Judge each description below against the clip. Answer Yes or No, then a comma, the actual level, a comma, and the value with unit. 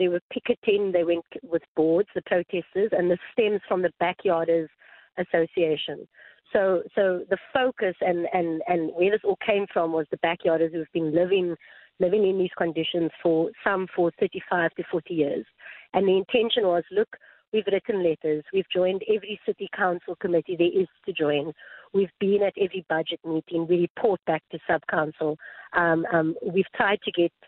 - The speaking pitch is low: No, medium, 180 Hz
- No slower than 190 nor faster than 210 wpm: No, average, 180 wpm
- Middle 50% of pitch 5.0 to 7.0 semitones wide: No, average, 2.9 semitones